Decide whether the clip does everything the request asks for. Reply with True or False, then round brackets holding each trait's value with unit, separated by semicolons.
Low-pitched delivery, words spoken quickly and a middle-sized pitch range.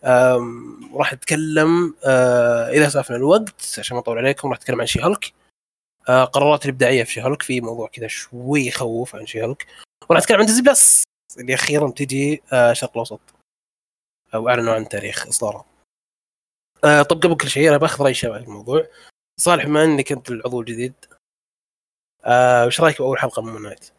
True (130 Hz; 175 wpm; 3.8 semitones)